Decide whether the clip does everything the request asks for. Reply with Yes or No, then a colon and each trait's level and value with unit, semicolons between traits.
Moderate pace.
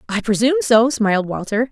Yes: average, 175 wpm